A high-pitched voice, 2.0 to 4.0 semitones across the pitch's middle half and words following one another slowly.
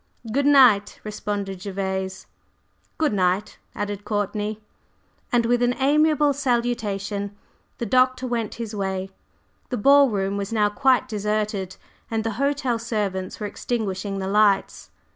Yes: high, 210 Hz; average, 3.5 semitones; slow, 130 wpm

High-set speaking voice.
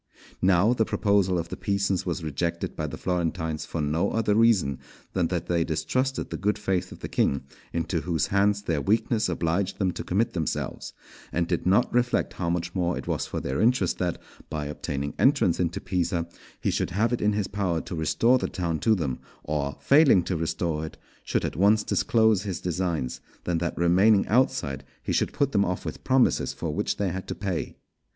No: very low, 90 Hz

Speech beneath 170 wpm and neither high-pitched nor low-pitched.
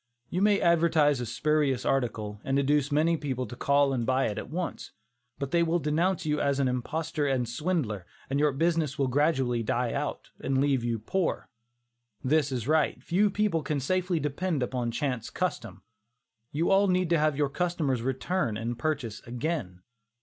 No: average, 175 wpm; medium, 145 Hz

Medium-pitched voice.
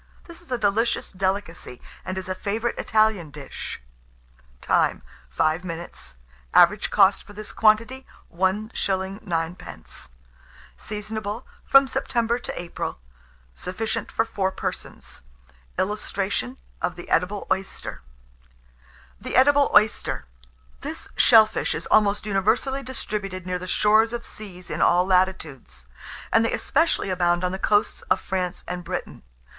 No: high, 200 Hz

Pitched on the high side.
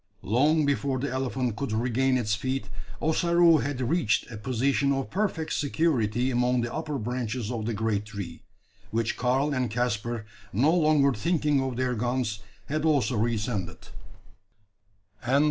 No: low, 125 Hz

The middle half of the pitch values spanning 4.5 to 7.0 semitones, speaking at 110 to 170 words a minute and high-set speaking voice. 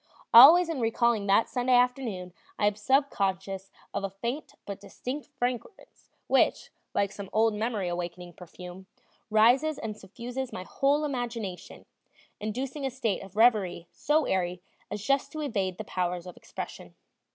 Yes: average, 5.2 semitones; average, 150 wpm; high, 220 Hz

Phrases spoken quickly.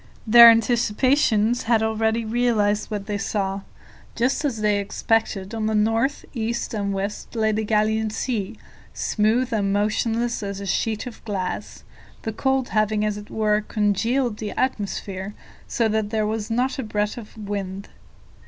No: average, 155 wpm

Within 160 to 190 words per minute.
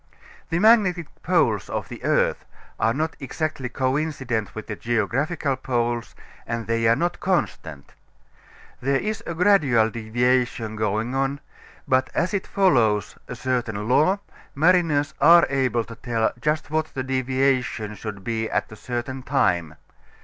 No: average, 140 wpm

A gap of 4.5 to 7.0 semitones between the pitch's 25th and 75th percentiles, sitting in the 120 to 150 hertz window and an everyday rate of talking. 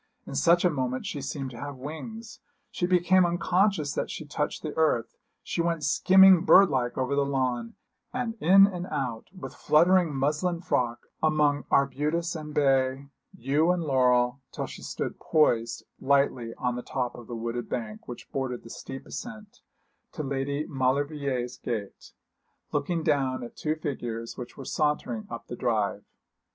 Yes: average, 4.8 semitones; medium, 140 Hz; average, 165 wpm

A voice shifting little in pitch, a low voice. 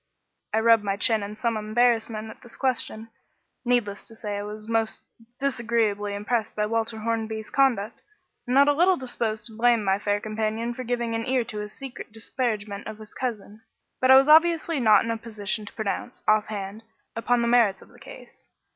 No: narrow, 2.3 semitones; high, 225 Hz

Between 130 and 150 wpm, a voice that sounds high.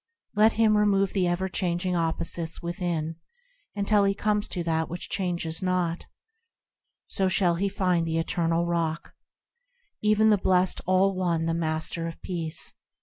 No: average, 145 wpm; medium, 180 Hz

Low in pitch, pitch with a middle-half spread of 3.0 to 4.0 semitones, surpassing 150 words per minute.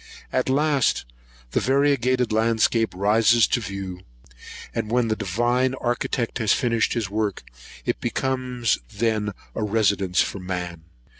No: low, 115 Hz; average, 3.4 semitones; slow, 135 wpm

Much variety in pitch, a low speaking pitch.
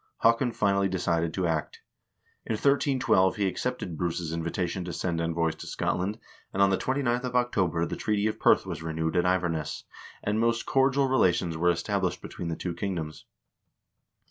No: average, 5.0 semitones; very low, 95 Hz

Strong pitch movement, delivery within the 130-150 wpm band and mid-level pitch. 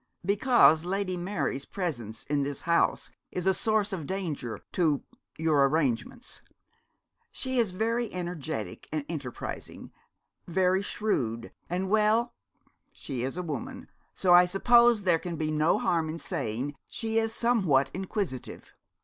Yes: wide, 6.0 semitones; slow, 135 wpm; medium, 175 Hz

